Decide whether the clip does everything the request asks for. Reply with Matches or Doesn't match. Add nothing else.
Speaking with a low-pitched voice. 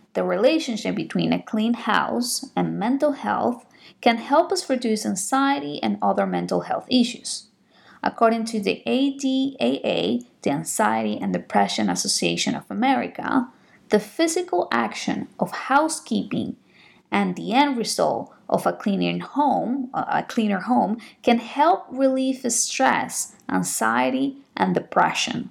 Doesn't match